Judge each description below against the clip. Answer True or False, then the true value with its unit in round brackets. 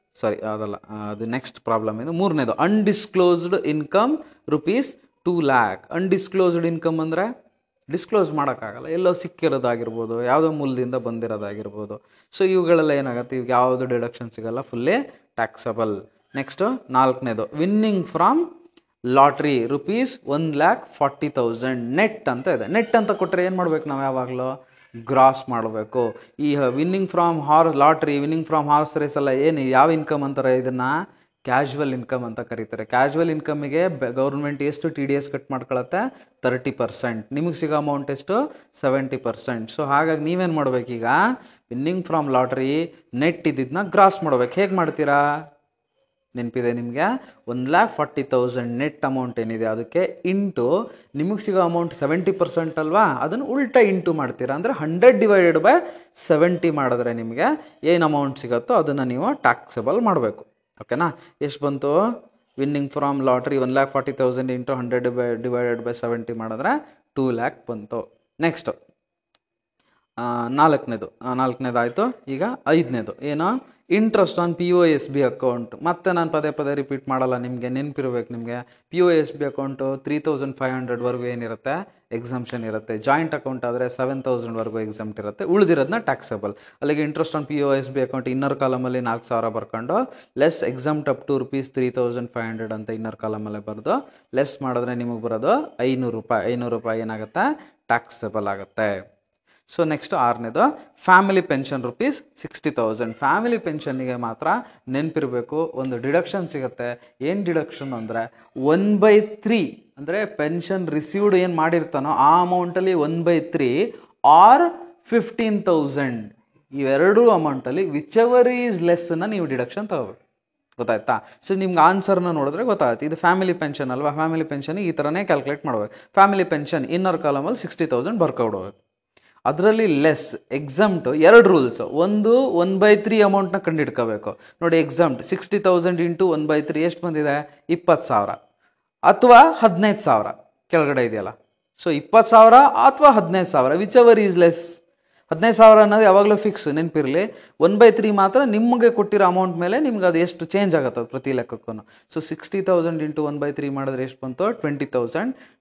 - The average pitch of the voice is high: False (150 Hz)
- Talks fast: True (145 wpm)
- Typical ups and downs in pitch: False (5.9 semitones)